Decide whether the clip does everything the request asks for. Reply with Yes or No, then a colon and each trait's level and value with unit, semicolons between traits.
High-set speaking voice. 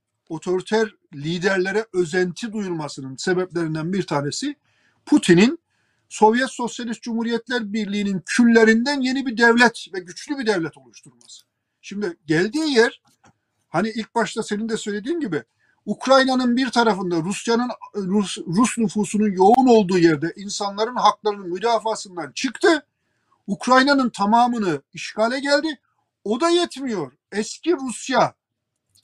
Yes: high, 215 Hz